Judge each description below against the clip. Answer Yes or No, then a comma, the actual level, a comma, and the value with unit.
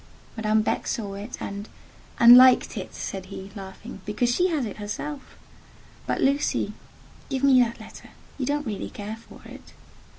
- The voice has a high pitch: Yes, high, 230 Hz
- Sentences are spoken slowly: No, average, 160 wpm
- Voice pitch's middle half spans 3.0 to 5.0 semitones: Yes, average, 4.3 semitones